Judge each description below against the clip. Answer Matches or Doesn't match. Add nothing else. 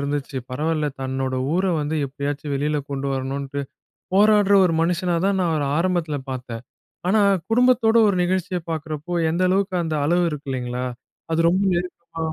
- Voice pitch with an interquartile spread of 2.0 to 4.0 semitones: Doesn't match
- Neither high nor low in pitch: Matches